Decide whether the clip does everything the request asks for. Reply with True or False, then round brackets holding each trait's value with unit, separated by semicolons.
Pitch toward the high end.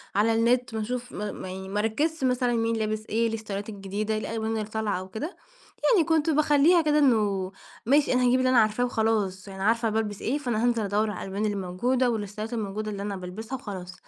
True (220 Hz)